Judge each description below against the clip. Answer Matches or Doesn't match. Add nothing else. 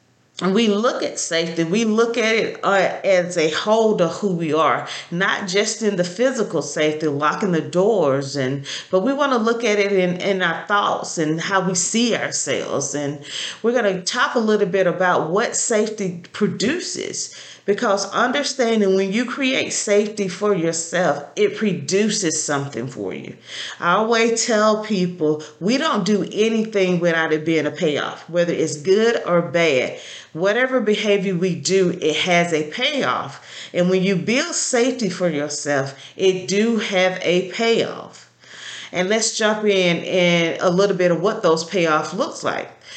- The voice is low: Doesn't match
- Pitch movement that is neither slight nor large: Matches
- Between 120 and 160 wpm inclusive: Doesn't match